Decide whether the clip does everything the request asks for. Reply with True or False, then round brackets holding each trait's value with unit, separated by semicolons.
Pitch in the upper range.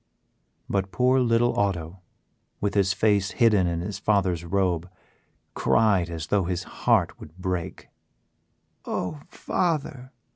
False (95 Hz)